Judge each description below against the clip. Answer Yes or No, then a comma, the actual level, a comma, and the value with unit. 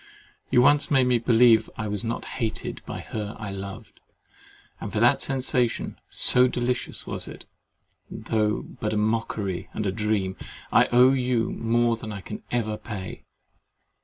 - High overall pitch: No, low, 115 Hz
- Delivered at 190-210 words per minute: No, average, 160 wpm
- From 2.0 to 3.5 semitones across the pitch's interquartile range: Yes, narrow, 2.6 semitones